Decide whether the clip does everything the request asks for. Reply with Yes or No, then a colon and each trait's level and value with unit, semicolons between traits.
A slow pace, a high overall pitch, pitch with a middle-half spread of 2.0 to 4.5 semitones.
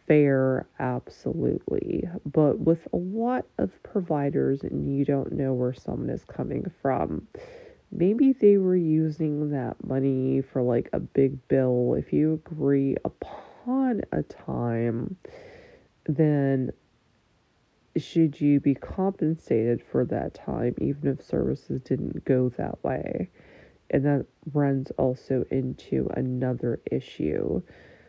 No: slow, 120 wpm; medium, 140 Hz; average, 4.1 semitones